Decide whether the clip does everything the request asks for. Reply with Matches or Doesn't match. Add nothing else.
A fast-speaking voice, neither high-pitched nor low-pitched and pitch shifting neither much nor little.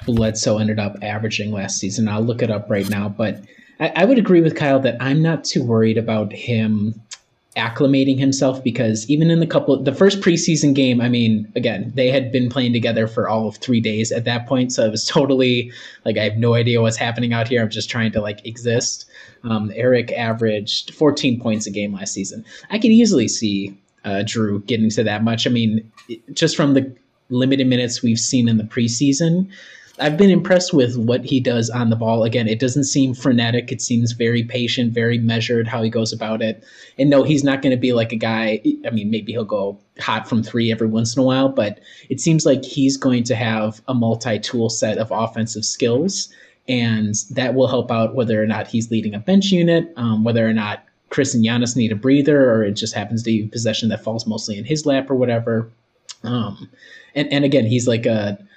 Doesn't match